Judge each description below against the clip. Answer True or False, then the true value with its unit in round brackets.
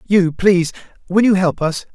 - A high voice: False (180 Hz)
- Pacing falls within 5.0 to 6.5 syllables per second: True (5.1 syllables/s)